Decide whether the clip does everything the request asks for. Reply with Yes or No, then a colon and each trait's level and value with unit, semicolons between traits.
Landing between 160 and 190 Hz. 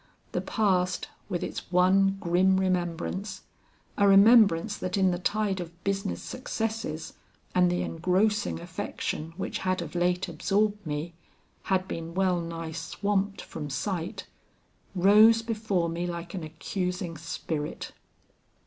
Yes: medium, 185 Hz